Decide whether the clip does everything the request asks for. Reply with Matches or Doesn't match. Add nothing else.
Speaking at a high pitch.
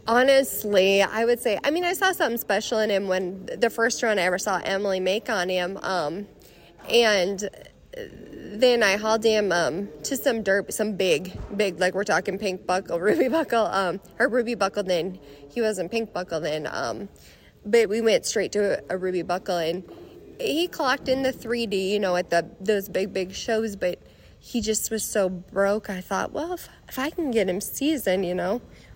Matches